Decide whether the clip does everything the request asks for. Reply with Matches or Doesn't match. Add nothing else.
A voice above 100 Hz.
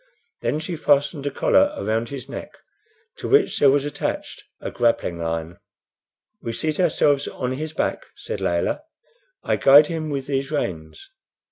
Matches